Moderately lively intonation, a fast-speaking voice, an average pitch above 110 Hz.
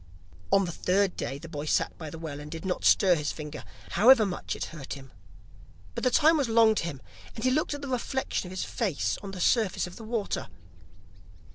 No: wide, 6.4 semitones; fast, 225 wpm; high, 190 Hz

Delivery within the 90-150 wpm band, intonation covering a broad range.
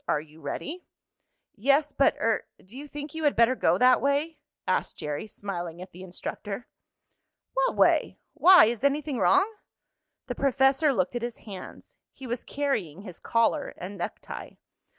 No: average, 160 wpm; wide, 7.1 semitones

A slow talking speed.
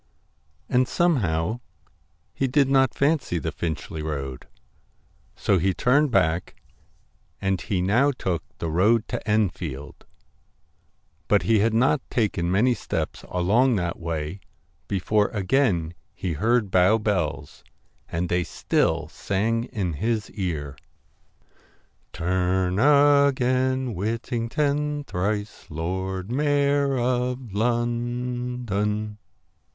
Yes: slow, 105 wpm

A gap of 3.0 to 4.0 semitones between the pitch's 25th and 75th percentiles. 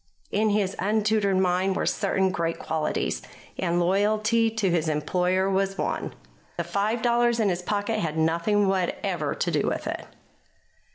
Yes: average, 3.3 semitones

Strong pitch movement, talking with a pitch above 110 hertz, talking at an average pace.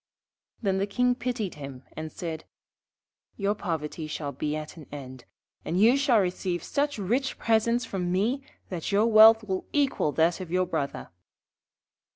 Yes: wide, 6.0 semitones; high, 190 Hz; average, 160 wpm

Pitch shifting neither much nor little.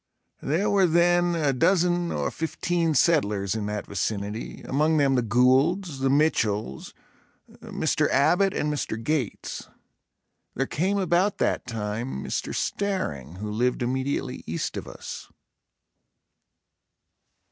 No: wide, 7.7 semitones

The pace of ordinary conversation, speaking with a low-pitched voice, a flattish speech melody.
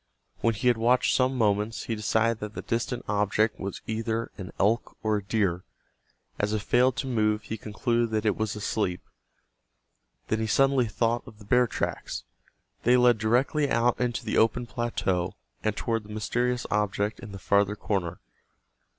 Yes: average, 175 wpm; low, 110 Hz; narrow, 2.3 semitones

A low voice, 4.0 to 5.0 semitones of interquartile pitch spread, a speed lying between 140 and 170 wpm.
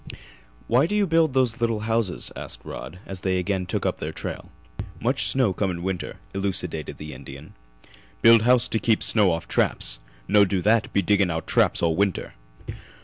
No: low, 100 Hz; average, 4.4 semitones; average, 185 wpm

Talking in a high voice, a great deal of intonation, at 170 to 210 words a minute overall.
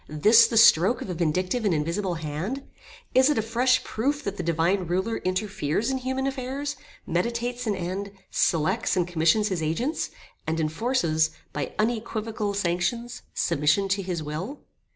No: high, 200 Hz; wide, 6.1 semitones; average, 155 wpm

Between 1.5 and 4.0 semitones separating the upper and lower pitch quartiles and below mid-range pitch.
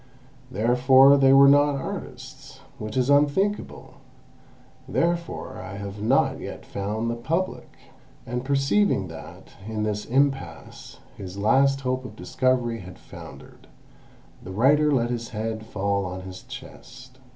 No: average, 4.5 semitones; low, 125 Hz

